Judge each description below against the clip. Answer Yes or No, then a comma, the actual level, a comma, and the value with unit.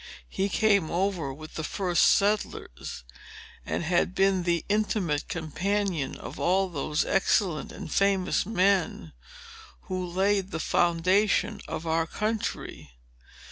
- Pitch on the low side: No, medium, 185 Hz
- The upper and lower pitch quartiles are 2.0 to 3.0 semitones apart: No, average, 3.4 semitones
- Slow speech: Yes, slow, 120 wpm